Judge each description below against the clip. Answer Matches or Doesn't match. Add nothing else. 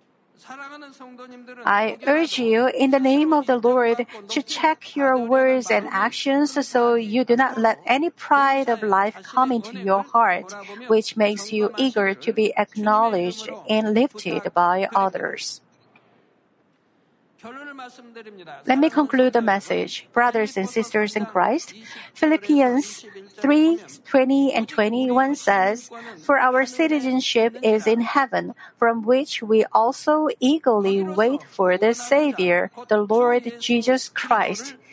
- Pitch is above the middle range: Matches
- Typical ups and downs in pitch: Matches